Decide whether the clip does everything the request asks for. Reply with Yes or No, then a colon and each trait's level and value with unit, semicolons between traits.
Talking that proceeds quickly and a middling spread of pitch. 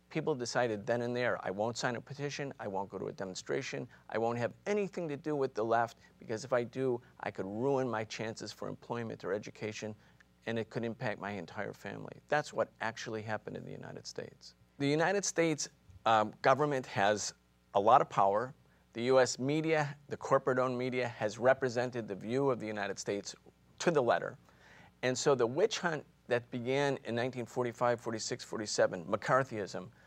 No: average, 185 wpm; average, 3.6 semitones